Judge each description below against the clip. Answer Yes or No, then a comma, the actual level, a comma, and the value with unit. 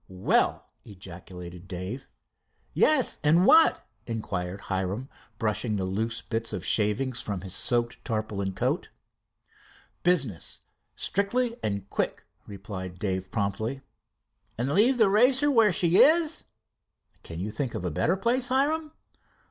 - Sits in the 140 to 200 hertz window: No, low, 115 Hz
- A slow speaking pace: Yes, slow, 125 wpm